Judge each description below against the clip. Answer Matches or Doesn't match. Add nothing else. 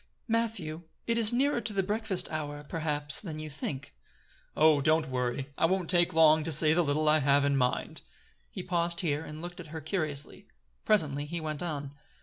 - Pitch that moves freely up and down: Doesn't match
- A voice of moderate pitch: Matches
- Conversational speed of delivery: Matches